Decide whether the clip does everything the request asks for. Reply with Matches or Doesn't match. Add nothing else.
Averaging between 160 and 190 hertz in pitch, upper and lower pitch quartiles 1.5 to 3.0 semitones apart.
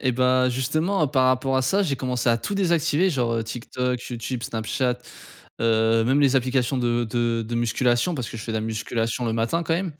Doesn't match